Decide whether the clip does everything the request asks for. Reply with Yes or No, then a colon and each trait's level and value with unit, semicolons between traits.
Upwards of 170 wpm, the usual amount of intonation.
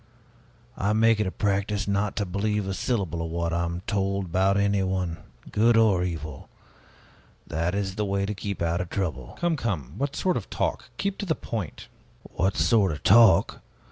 Yes: average, 185 wpm; average, 3.3 semitones